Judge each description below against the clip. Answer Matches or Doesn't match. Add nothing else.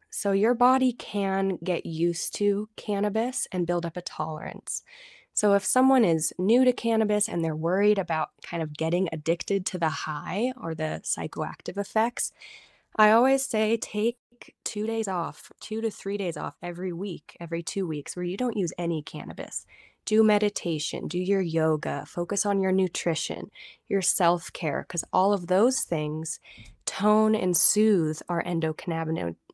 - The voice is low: Doesn't match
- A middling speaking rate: Matches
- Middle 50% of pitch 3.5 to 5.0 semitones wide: Matches